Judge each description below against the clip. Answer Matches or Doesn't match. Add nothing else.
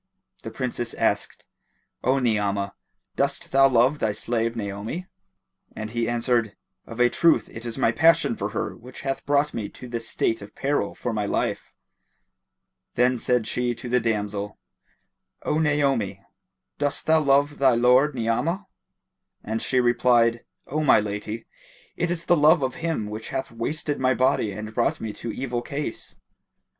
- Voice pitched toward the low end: Matches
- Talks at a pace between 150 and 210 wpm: Matches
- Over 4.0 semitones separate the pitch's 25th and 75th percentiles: Doesn't match